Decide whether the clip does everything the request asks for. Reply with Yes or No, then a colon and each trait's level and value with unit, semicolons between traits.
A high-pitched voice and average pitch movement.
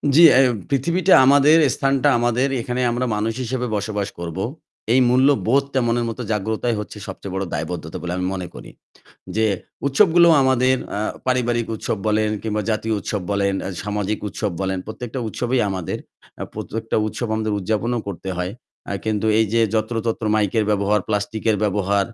No: low, 110 Hz; average, 3.5 semitones